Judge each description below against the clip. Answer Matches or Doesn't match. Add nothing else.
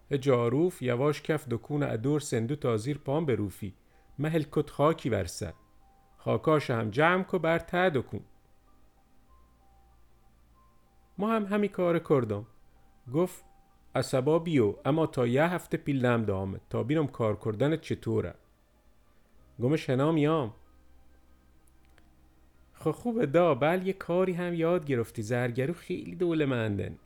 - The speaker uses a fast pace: Doesn't match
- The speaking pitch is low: Matches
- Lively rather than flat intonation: Matches